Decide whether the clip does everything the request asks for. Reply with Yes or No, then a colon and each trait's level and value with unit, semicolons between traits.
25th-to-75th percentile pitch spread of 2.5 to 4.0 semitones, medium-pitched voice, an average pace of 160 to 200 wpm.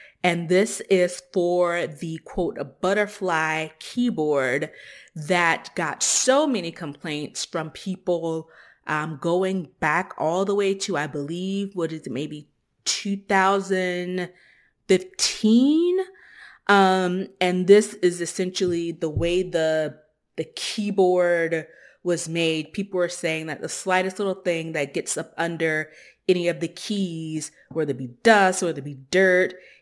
No: average, 2.9 semitones; medium, 175 Hz; slow, 135 wpm